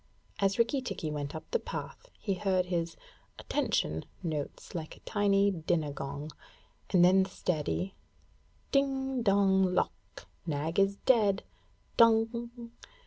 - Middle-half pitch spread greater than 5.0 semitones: Yes, wide, 5.6 semitones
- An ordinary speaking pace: No, slow, 130 wpm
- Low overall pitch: No, high, 195 Hz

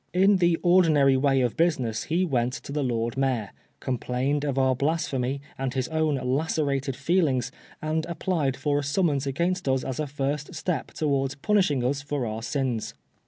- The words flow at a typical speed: Yes, average, 170 wpm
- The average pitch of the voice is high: No, medium, 140 Hz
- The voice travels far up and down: No, average, 3.3 semitones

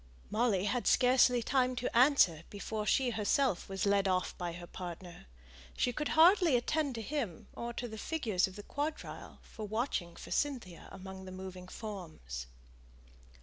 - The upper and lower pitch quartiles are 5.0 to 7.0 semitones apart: Yes, wide, 5.4 semitones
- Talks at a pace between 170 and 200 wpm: No, average, 160 wpm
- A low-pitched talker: No, high, 215 Hz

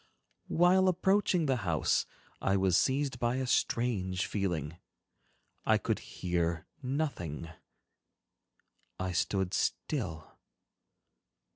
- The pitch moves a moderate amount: No, wide, 7.6 semitones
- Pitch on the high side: No, low, 100 Hz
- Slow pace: Yes, slow, 95 wpm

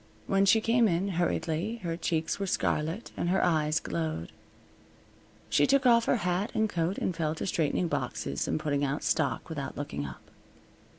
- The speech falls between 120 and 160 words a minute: No, average, 175 wpm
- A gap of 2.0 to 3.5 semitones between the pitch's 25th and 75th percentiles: No, average, 4.6 semitones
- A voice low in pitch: No, medium, 165 Hz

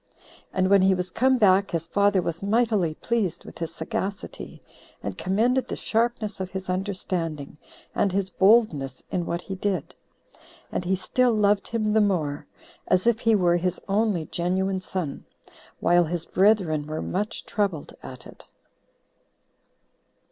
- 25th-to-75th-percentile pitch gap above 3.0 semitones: Yes, average, 3.4 semitones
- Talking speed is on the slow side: No, average, 150 wpm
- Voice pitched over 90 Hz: Yes, high, 190 Hz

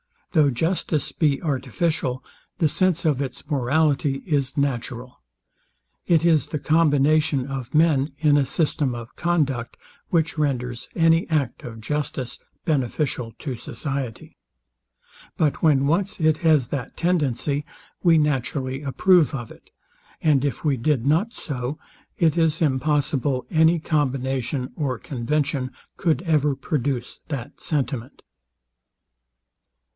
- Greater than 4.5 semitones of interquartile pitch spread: No, average, 3.3 semitones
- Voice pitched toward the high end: No, medium, 145 Hz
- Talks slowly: Yes, slow, 120 wpm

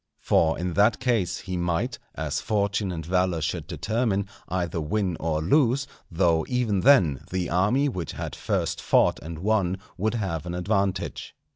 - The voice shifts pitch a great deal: No, average, 4.2 semitones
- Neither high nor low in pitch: No, very low, 95 Hz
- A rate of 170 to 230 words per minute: No, average, 160 wpm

